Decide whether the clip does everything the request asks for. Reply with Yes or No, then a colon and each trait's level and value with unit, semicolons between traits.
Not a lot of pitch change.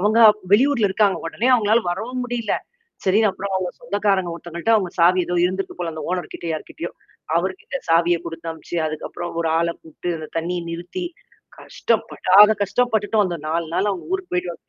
No: average, 3.8 semitones